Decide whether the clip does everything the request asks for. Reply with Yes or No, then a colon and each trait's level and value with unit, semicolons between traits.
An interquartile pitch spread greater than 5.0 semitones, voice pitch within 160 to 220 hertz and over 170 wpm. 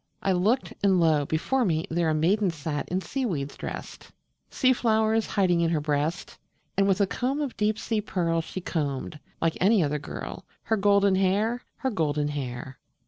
Yes: wide, 5.4 semitones; medium, 185 Hz; average, 180 wpm